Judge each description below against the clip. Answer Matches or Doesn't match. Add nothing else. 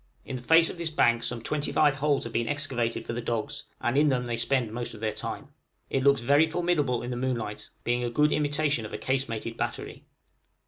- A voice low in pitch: Matches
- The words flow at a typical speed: Doesn't match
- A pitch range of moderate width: Matches